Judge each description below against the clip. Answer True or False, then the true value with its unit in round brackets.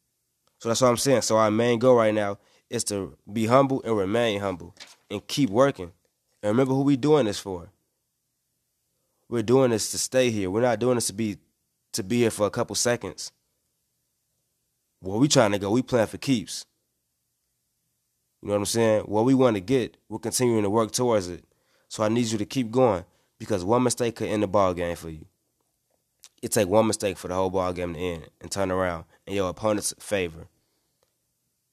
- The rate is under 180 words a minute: False (200 wpm)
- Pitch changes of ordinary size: True (4.1 semitones)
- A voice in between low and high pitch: False (110 Hz)